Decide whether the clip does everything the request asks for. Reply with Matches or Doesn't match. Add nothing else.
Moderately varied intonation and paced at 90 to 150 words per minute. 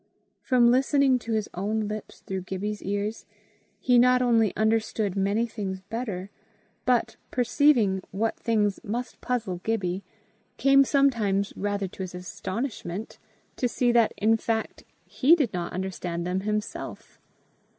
Matches